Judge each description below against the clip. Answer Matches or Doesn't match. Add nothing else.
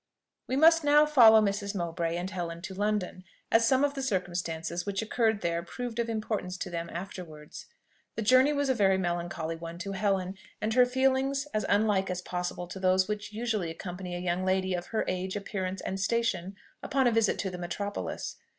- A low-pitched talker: Doesn't match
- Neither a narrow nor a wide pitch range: Matches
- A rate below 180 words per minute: Doesn't match